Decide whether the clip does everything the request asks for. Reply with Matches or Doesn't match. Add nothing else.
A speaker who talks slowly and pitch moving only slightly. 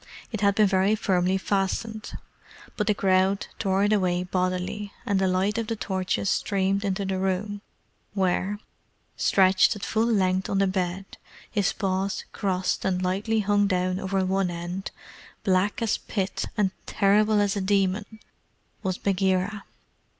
Doesn't match